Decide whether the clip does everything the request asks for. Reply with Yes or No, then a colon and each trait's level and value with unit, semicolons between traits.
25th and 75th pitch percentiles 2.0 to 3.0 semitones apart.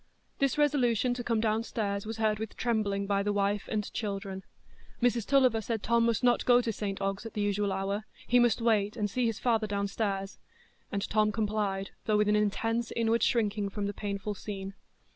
Yes: narrow, 2.4 semitones